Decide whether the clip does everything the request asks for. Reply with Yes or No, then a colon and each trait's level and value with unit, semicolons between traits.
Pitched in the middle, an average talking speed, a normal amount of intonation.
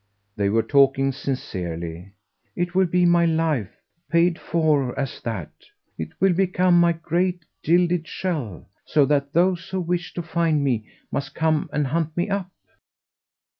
Yes: medium, 160 Hz; average, 150 wpm; average, 4.3 semitones